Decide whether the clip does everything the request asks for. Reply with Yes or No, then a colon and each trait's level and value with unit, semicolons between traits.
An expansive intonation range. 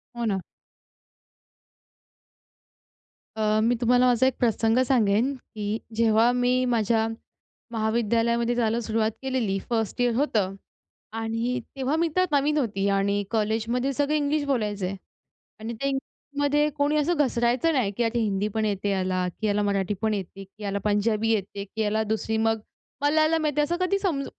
No: average, 3.9 semitones